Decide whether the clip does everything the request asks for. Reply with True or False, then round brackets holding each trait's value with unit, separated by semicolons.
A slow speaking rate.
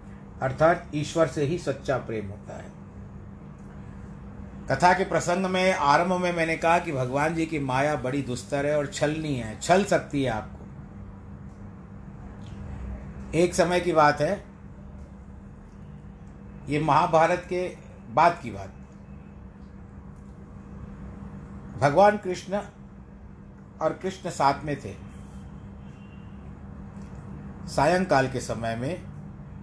True (105 wpm)